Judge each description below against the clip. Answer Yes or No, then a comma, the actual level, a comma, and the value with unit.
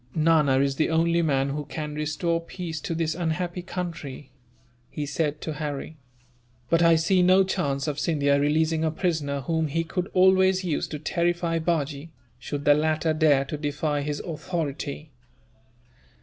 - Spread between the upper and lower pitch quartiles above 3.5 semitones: No, narrow, 2.5 semitones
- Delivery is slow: No, average, 160 wpm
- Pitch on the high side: No, medium, 155 Hz